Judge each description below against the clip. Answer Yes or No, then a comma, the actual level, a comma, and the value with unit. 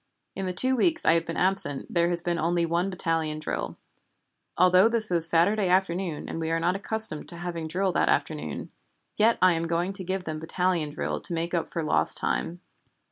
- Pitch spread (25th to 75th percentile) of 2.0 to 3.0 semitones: Yes, narrow, 2.4 semitones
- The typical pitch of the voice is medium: Yes, medium, 175 Hz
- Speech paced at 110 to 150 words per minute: No, fast, 205 wpm